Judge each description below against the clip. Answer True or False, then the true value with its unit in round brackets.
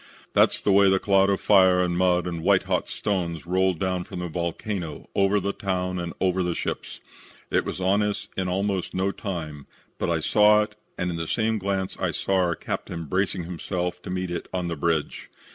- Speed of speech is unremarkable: False (210 wpm)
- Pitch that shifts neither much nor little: False (2.1 semitones)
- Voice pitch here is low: True (90 Hz)